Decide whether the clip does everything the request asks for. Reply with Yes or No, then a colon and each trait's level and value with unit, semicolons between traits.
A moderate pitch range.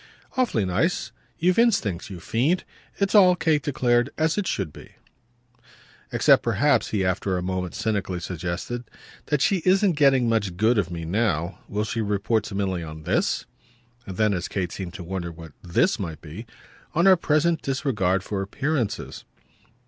No: wide, 8.3 semitones